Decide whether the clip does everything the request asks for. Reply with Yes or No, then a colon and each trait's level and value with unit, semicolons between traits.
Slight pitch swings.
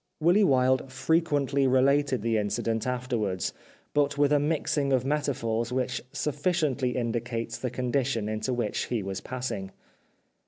No: average, 3.6 semitones